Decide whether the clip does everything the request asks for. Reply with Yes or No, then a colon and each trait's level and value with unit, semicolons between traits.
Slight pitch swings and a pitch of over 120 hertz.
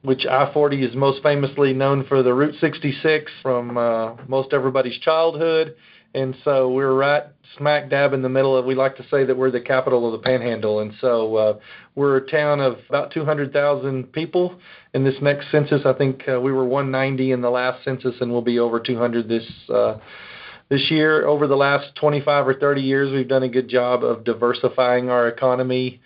Yes: narrow, 2.0 semitones; low, 135 Hz